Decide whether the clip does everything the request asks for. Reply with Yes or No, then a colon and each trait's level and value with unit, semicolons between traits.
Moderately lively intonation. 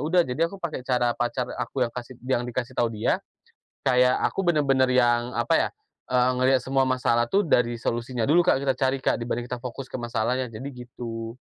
No: narrow, 1.9 semitones